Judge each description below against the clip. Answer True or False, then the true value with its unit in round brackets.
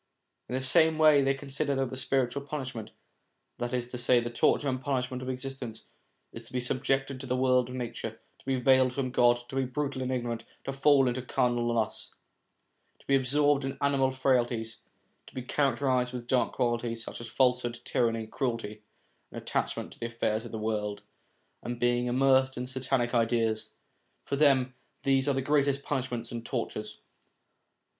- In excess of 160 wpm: True (180 wpm)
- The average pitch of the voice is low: True (125 Hz)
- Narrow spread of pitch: True (2.1 semitones)